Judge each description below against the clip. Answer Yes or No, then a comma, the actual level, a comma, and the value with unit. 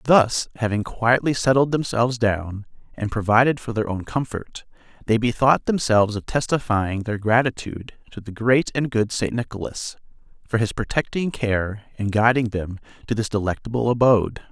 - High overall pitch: No, low, 115 Hz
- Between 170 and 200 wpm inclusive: No, average, 155 wpm